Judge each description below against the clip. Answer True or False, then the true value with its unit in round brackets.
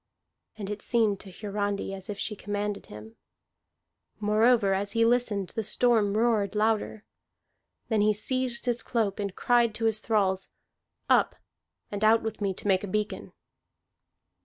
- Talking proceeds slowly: False (155 wpm)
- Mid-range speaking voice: False (210 Hz)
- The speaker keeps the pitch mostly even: True (2.1 semitones)